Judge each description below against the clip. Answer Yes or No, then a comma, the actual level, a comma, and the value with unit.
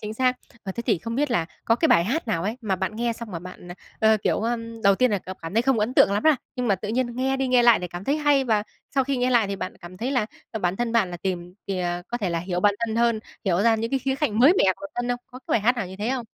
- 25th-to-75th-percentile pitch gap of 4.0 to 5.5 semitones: Yes, average, 4.6 semitones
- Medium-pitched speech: No, high, 225 Hz